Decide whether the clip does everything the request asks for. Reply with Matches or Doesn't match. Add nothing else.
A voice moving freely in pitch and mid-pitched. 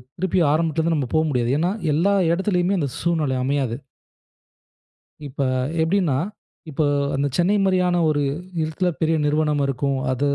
Doesn't match